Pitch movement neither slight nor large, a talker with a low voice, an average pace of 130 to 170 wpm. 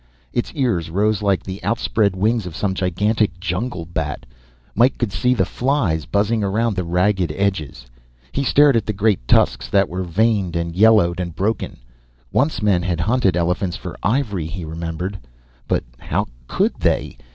Yes: average, 4.2 semitones; very low, 95 Hz; average, 165 wpm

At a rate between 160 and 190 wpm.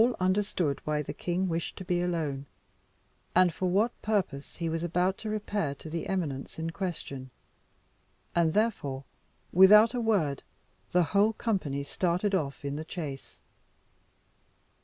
No: average, 145 wpm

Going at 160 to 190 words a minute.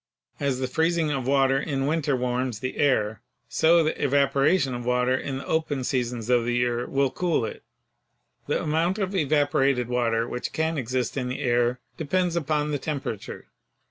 Yes: average, 175 wpm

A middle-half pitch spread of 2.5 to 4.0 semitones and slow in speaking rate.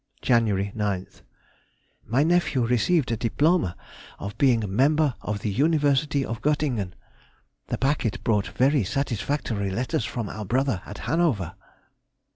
No: wide, 5.6 semitones; slow, 120 wpm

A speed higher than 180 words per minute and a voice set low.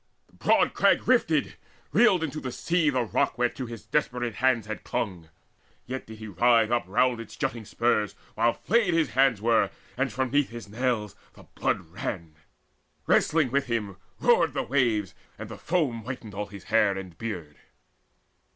No: average, 170 wpm; low, 120 Hz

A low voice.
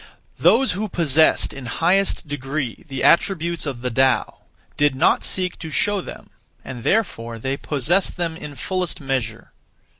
No: medium, 150 Hz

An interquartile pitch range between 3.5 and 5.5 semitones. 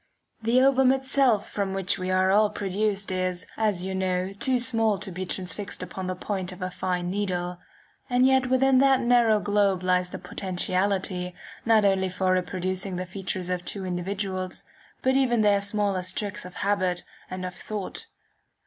No: average, 2.7 semitones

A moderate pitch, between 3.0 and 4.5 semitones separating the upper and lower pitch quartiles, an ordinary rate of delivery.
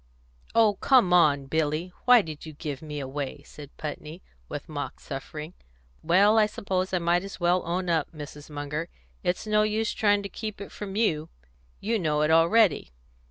No: medium, 175 Hz; average, 5.2 semitones; average, 175 wpm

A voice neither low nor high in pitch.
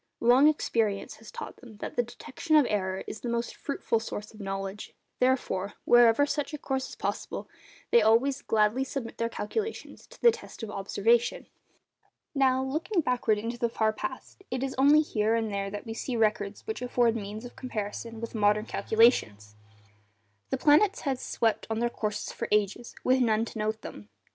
No: high, 230 Hz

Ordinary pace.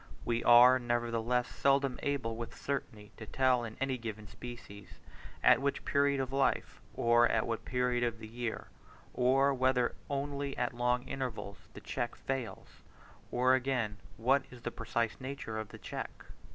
Yes: average, 160 wpm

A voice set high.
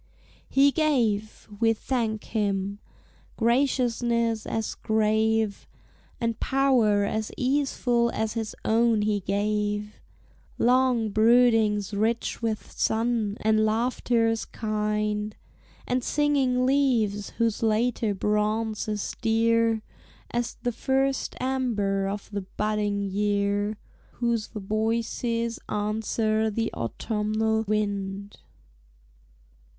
Yes: high, 220 Hz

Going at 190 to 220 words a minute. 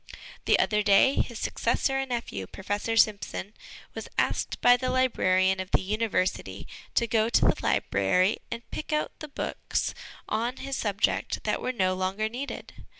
No: average, 160 wpm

